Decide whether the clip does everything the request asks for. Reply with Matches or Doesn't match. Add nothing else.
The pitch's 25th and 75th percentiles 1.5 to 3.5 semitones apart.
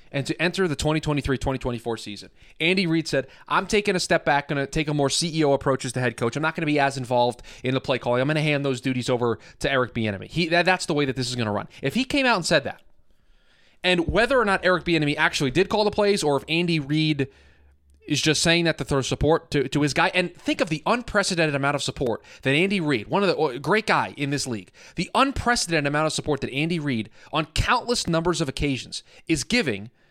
Doesn't match